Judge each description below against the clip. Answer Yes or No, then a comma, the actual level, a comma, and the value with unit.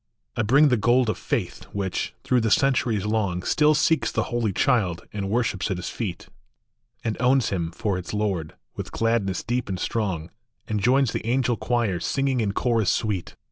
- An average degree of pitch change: Yes, average, 4.2 semitones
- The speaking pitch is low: Yes, low, 110 Hz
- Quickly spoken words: No, average, 180 wpm